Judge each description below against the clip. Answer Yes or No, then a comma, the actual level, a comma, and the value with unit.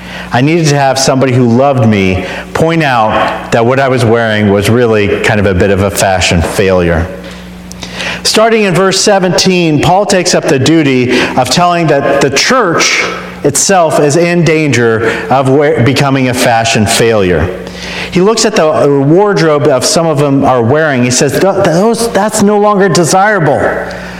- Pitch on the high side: No, medium, 140 Hz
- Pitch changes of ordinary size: No, wide, 7.4 semitones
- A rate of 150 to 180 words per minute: Yes, average, 170 wpm